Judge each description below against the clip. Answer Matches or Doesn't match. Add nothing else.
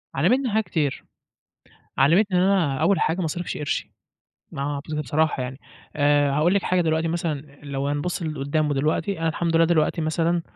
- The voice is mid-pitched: Matches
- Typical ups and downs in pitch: Matches